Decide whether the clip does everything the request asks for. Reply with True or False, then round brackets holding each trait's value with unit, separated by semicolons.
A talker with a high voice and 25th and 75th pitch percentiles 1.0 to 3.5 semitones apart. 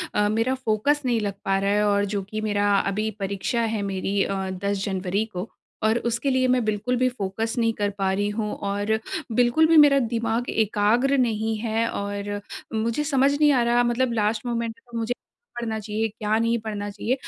True (220 Hz; 2.8 semitones)